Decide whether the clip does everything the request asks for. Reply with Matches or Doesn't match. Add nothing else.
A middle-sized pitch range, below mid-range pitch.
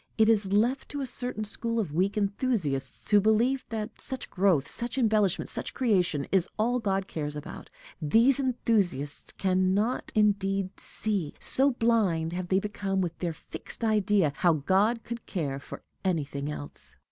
Doesn't match